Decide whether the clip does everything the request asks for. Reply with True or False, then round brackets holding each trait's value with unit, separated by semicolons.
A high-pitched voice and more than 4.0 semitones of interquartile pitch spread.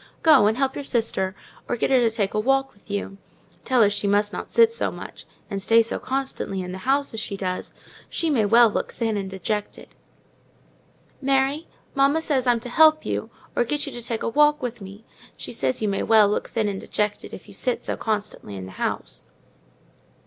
True (225 Hz; 4.9 semitones)